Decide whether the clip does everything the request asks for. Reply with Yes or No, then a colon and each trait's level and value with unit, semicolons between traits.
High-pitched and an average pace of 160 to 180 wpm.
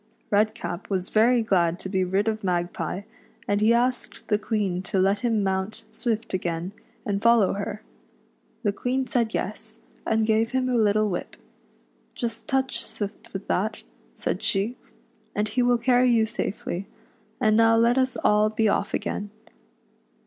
Yes: high, 215 Hz; average, 170 wpm